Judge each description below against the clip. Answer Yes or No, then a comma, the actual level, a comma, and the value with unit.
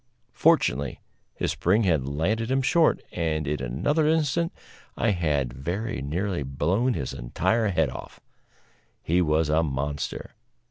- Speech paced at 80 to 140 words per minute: Yes, slow, 135 wpm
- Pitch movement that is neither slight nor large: No, wide, 7.7 semitones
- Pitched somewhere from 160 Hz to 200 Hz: No, very low, 85 Hz